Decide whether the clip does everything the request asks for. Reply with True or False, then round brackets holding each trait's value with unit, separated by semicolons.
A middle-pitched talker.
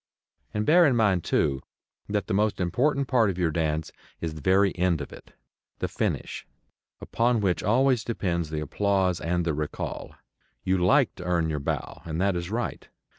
False (95 Hz)